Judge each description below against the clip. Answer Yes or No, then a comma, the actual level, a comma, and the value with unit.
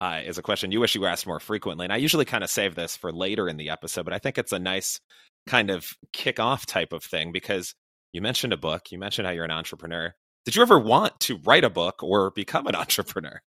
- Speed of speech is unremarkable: No, fast, 260 wpm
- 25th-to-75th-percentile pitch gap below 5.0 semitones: Yes, average, 3.4 semitones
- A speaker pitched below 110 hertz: Yes, very low, 90 Hz